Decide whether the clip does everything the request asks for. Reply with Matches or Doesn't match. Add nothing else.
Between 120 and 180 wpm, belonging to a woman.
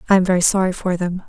Doesn't match